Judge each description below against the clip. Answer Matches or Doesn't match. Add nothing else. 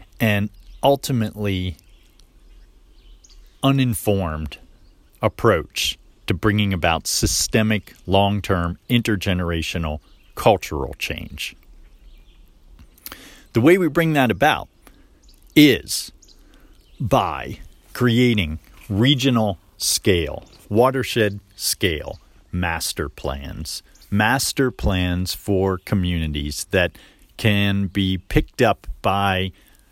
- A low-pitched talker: Matches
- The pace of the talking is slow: Matches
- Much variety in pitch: Doesn't match